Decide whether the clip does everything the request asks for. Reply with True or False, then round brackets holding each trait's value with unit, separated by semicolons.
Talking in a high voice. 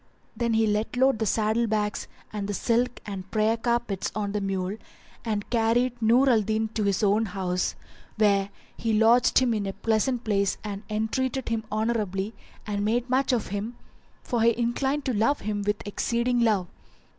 True (220 Hz)